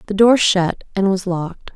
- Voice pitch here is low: No, high, 195 Hz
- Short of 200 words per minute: No, fast, 205 wpm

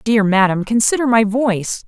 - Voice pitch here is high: Yes, high, 220 Hz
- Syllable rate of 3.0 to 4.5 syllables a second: No, 5.0 syllables/s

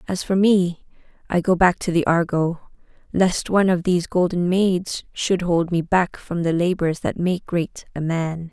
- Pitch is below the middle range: No, medium, 175 Hz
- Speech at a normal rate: Yes, average, 190 wpm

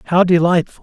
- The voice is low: No, medium, 175 Hz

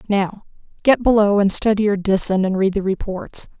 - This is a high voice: Yes, high, 200 Hz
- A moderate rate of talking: Yes, average, 185 wpm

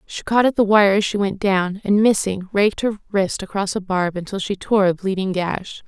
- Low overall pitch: No, high, 195 Hz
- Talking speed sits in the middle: No, fast, 235 wpm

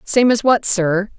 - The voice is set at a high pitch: Yes, high, 215 Hz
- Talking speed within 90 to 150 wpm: No, fast, 205 wpm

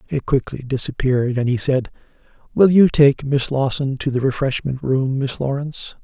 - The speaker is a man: Yes, male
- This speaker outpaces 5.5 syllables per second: No, 5.1 syllables/s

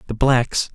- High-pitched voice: No, low, 125 Hz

